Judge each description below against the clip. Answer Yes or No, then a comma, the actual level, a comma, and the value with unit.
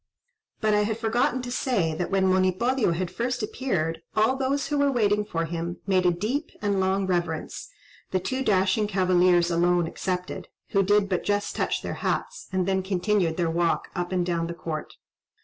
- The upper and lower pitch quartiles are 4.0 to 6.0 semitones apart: No, average, 3.4 semitones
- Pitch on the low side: No, high, 190 Hz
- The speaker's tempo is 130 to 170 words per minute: No, average, 185 wpm